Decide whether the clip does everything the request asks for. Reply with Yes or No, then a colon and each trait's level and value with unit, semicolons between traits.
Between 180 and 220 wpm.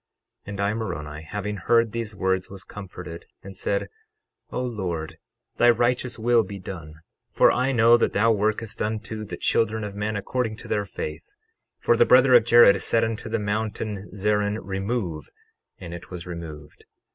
No: average, 170 wpm